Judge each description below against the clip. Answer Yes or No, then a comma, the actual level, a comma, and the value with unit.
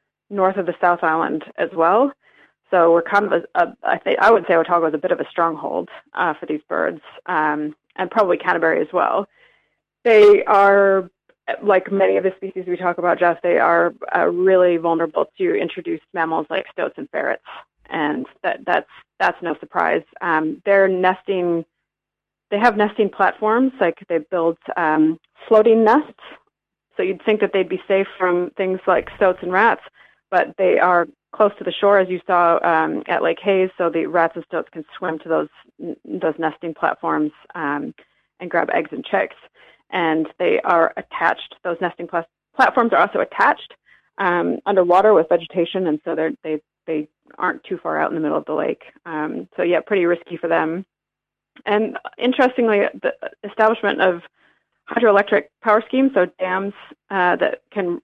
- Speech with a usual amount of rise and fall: Yes, average, 3.3 semitones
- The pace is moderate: Yes, average, 180 wpm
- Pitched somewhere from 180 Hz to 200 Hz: Yes, medium, 185 Hz